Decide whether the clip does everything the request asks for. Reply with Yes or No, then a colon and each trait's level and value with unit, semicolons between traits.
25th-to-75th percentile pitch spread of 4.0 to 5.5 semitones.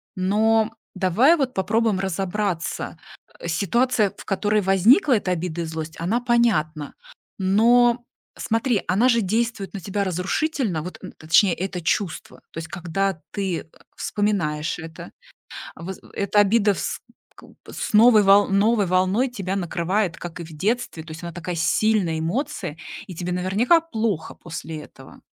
Yes: average, 4.3 semitones